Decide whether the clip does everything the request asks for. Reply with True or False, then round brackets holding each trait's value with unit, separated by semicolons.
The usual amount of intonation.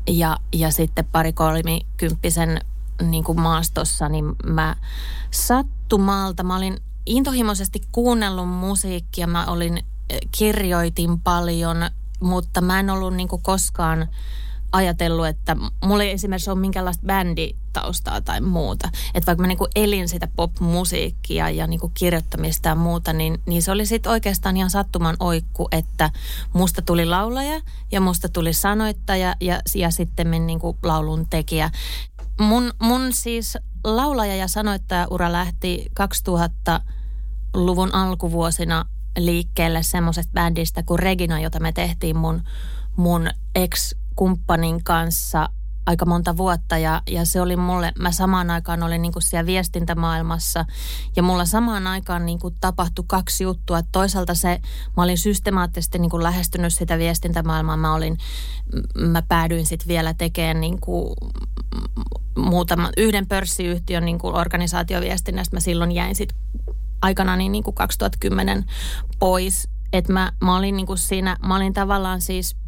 False (2.2 semitones)